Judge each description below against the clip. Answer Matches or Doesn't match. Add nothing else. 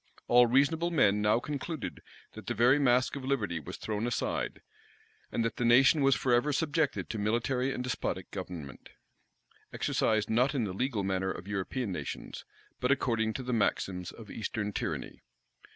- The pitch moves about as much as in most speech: Matches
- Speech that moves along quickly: Doesn't match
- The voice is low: Matches